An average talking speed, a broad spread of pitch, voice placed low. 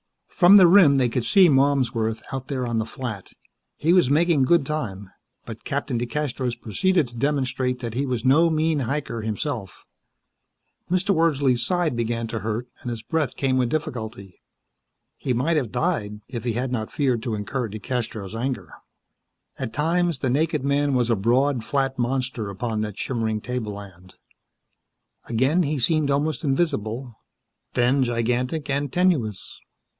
No: average, 155 wpm; average, 4.3 semitones; low, 130 Hz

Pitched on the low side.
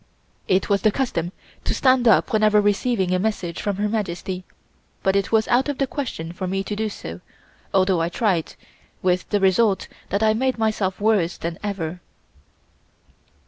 No: high, 200 Hz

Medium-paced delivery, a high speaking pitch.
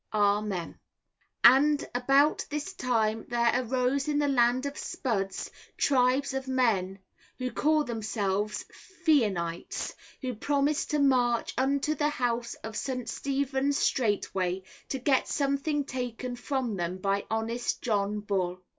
No: slow, 130 wpm; high, 245 Hz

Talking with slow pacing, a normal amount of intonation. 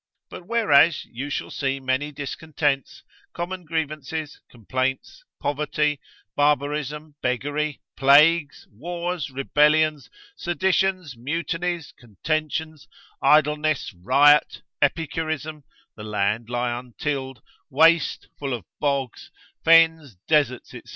Yes: slow, 95 wpm; average, 3.1 semitones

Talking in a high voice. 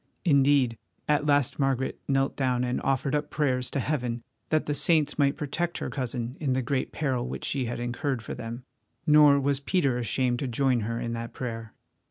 No: low, 135 Hz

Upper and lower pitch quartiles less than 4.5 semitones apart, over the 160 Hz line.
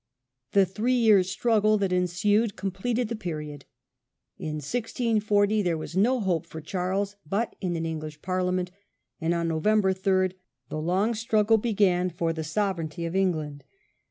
Yes: average, 4.1 semitones; high, 190 Hz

